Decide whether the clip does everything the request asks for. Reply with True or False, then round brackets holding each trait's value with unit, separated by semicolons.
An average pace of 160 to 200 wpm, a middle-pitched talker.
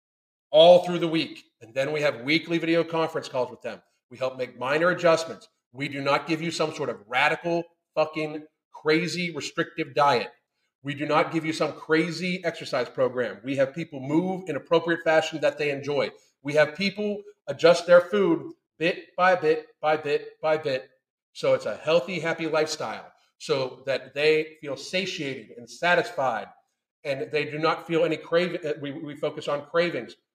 True (175 wpm; 160 Hz)